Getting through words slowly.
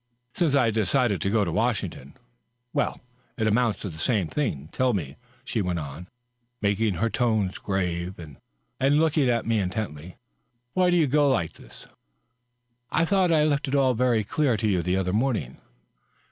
No: average, 190 wpm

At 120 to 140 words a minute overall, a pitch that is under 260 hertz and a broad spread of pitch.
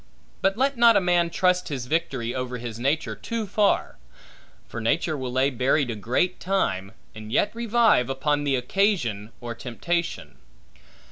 No: average, 155 wpm; medium, 140 Hz; wide, 7.4 semitones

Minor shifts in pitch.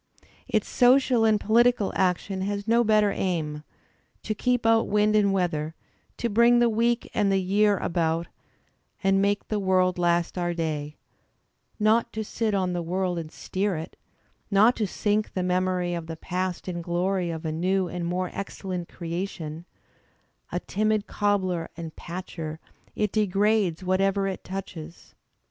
No: average, 3.3 semitones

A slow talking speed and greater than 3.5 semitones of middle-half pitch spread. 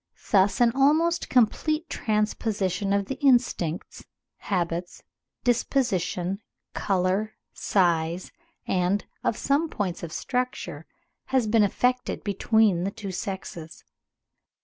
Yes: slow, 100 wpm; average, 5.1 semitones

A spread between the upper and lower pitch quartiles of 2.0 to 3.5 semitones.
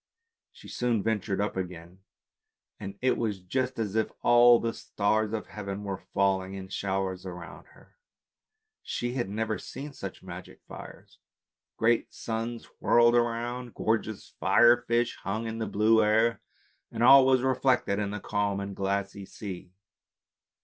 Yes: average, 3.2 semitones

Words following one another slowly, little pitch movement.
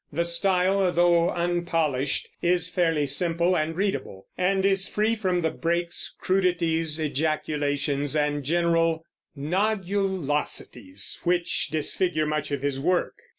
No: slow, 115 wpm; average, 3.2 semitones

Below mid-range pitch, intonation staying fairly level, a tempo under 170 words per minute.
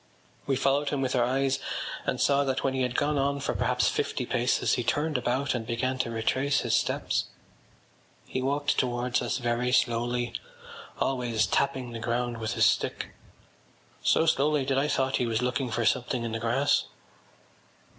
No: low, 125 Hz; narrow, 2.3 semitones; average, 175 wpm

